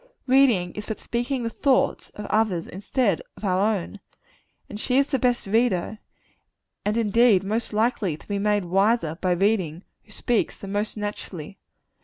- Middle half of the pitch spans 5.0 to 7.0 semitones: No, average, 3.4 semitones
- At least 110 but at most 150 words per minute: No, average, 165 wpm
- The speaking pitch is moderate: No, high, 210 Hz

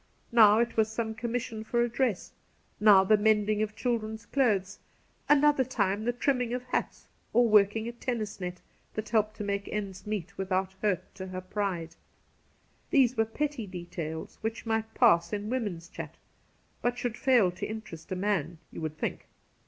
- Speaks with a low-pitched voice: No, high, 215 Hz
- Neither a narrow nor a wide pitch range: Yes, average, 3.6 semitones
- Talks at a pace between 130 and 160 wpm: No, average, 175 wpm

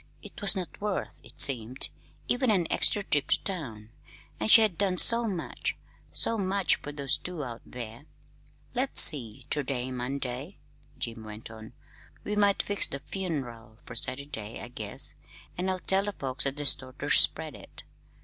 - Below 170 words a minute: No, average, 175 wpm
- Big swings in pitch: Yes, wide, 7.8 semitones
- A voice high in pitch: No, medium, 145 Hz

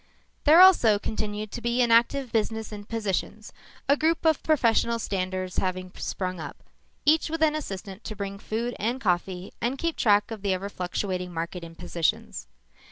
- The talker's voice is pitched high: Yes, high, 210 Hz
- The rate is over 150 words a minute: Yes, average, 170 wpm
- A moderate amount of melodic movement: Yes, average, 4.6 semitones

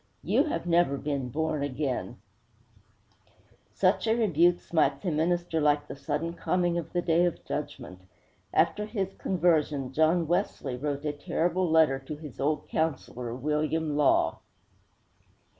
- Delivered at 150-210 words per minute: No, average, 140 wpm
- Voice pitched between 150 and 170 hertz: Yes, medium, 155 Hz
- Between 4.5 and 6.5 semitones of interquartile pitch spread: No, average, 3.3 semitones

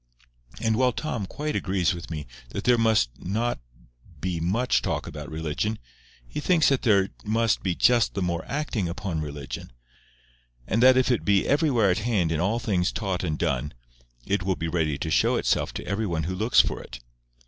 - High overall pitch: No, low, 100 Hz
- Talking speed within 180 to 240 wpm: Yes, average, 190 wpm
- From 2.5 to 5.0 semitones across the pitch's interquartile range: No, wide, 5.4 semitones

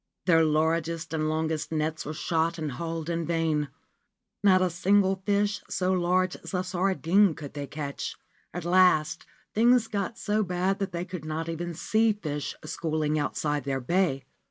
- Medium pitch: Yes, medium, 170 Hz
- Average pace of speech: Yes, average, 165 wpm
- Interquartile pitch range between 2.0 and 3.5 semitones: Yes, average, 3.1 semitones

